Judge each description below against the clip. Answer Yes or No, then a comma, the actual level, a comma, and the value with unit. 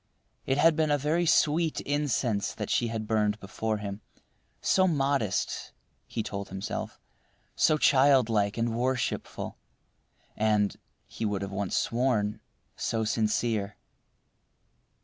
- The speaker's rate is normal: No, slow, 120 wpm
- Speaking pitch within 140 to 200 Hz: No, low, 115 Hz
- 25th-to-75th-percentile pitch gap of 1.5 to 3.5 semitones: No, average, 5.2 semitones